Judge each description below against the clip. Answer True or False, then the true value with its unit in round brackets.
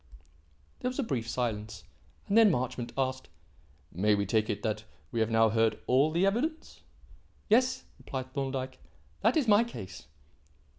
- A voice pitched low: True (130 Hz)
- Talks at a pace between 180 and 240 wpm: False (155 wpm)